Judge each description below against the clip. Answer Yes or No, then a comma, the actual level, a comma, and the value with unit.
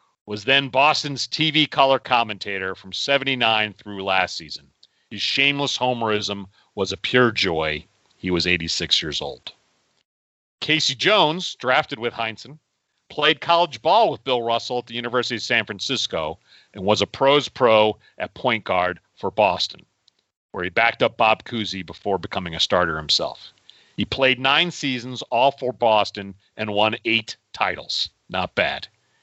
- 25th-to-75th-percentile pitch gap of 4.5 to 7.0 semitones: Yes, wide, 5.4 semitones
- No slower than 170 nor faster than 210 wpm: No, average, 150 wpm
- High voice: No, low, 115 Hz